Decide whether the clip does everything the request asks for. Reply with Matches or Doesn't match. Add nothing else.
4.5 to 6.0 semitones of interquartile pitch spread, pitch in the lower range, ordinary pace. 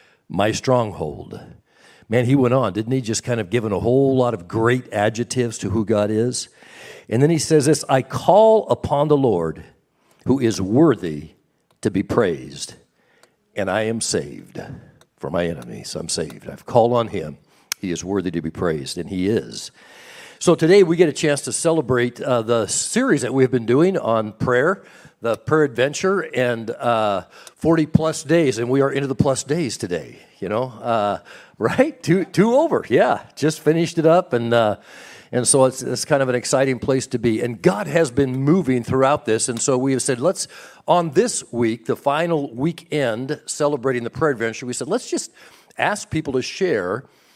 Matches